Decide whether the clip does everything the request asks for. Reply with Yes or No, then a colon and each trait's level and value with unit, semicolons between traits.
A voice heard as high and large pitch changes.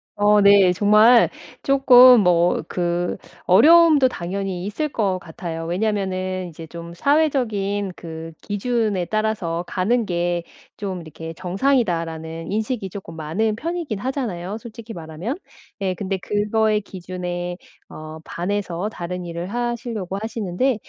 No: high, 195 Hz; average, 4.1 semitones